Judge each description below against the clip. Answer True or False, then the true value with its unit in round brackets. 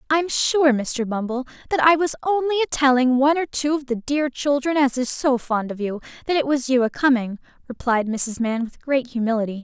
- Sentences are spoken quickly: True (220 wpm)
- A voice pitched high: True (265 Hz)